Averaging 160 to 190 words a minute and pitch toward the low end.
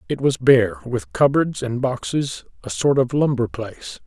Yes: average, 175 wpm; low, 130 Hz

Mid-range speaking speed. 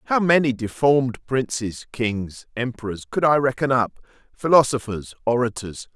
No: slow, 120 wpm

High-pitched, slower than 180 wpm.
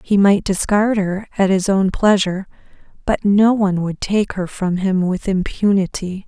Yes: high, 195 Hz; average, 170 wpm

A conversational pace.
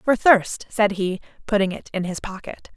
Yes: average, 195 wpm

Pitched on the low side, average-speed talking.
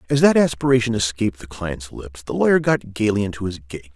No: low, 110 Hz; fast, 210 wpm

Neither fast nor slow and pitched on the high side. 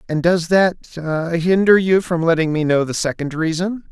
No: average, 185 wpm; medium, 170 Hz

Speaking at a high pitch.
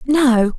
Yes: very high, 255 Hz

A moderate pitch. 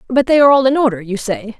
No: high, 240 Hz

